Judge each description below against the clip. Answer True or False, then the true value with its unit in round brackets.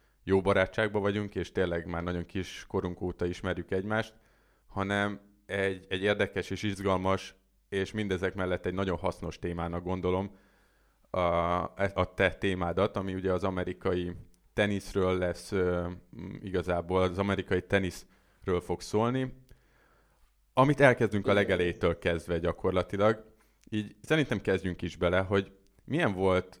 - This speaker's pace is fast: False (125 wpm)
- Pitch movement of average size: False (2.1 semitones)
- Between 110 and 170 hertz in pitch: False (95 Hz)